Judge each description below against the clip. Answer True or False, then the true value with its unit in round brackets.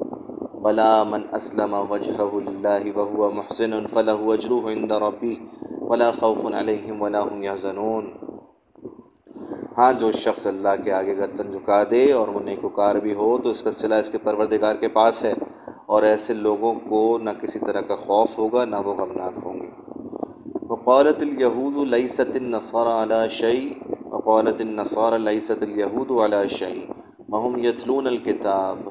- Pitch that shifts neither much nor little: False (1.8 semitones)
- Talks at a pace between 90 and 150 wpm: True (145 wpm)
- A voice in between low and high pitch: False (110 Hz)